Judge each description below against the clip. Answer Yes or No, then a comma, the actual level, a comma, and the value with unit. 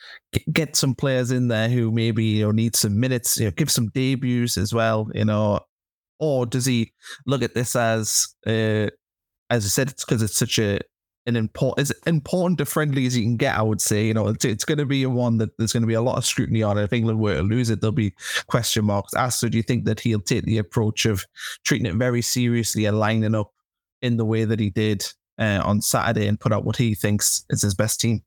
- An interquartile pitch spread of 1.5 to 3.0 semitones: Yes, narrow, 2.6 semitones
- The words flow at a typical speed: No, fast, 245 wpm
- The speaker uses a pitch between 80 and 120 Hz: Yes, low, 115 Hz